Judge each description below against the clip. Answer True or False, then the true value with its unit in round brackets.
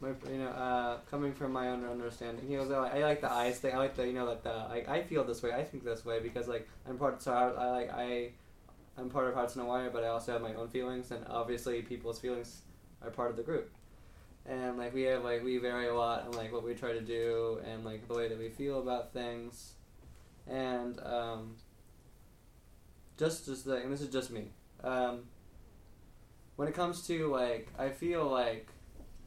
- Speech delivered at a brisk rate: True (225 wpm)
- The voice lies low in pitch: True (120 Hz)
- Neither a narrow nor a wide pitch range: False (1.7 semitones)